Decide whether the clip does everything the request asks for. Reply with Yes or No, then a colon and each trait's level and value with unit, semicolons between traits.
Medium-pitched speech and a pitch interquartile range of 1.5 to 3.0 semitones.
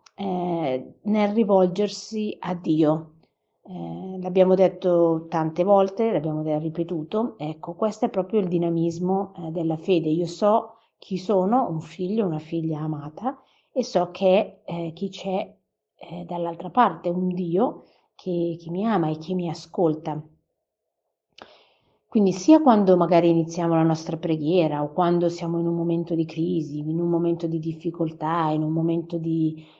Yes: medium, 170 Hz; narrow, 2.6 semitones